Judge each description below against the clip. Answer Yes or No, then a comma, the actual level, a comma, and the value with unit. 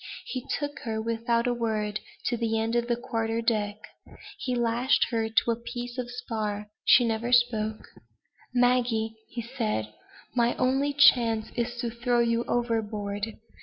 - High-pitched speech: Yes, high, 235 Hz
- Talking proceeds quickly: No, average, 155 wpm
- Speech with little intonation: Yes, narrow, 1.6 semitones